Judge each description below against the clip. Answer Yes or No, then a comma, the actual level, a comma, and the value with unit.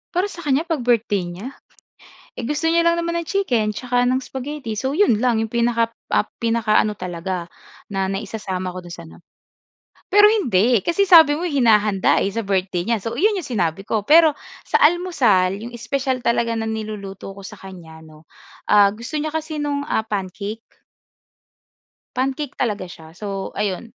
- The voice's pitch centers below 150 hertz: No, high, 230 Hz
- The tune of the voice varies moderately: No, wide, 6.7 semitones